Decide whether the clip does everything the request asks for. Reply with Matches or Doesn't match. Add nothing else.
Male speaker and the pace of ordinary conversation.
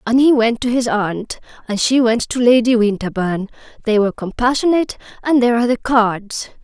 Doesn't match